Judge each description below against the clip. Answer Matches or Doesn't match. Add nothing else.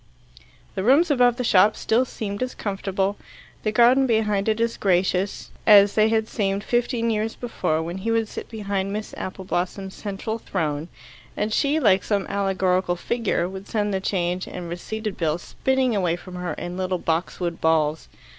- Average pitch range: Matches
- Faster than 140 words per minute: Matches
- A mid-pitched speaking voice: Doesn't match